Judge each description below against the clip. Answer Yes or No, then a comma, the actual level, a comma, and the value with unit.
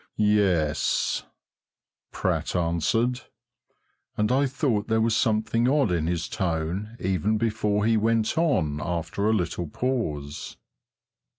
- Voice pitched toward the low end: Yes, low, 105 Hz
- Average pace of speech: No, slow, 115 wpm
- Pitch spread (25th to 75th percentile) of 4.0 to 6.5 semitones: Yes, average, 4.9 semitones